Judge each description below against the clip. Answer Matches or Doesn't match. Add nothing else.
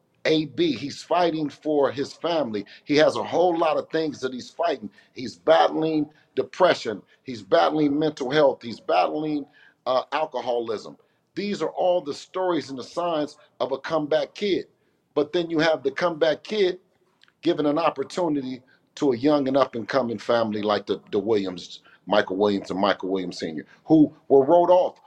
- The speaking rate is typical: Matches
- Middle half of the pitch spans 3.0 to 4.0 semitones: Doesn't match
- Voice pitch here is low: Doesn't match